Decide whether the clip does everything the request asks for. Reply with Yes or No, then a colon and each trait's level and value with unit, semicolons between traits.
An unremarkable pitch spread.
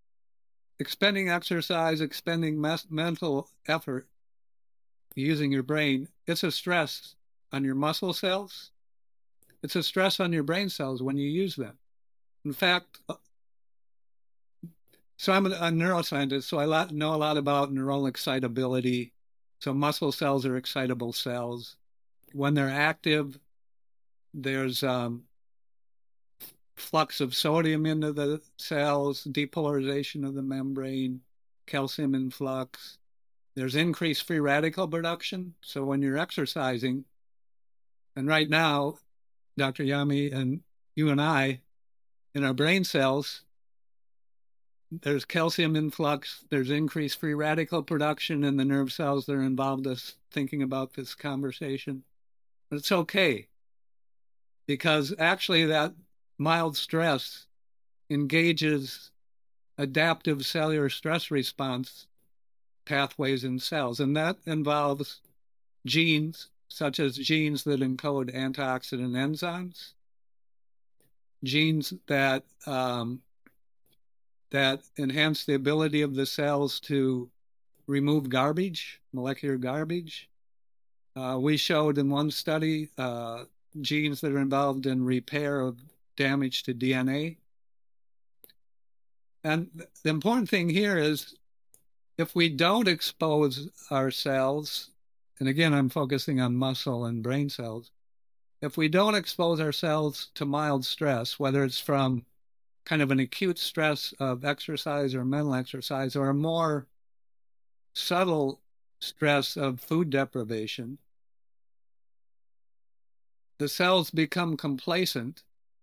Yes: average, 3.2 semitones